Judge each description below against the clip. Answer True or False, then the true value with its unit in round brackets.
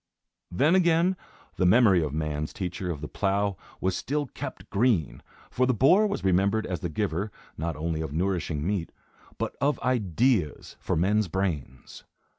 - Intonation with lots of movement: True (6.7 semitones)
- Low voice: True (95 Hz)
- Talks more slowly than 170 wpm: True (160 wpm)